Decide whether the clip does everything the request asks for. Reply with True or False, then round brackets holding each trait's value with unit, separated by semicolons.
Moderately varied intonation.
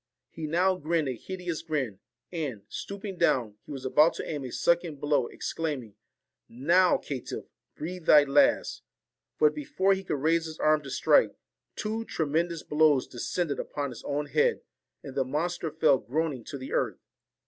True (4.1 semitones)